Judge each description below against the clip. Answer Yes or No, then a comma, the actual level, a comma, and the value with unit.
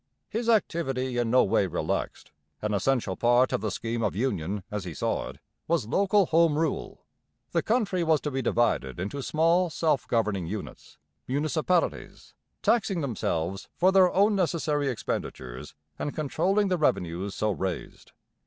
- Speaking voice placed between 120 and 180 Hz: Yes, low, 135 Hz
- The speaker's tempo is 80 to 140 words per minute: No, average, 155 wpm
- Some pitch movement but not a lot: No, wide, 8.4 semitones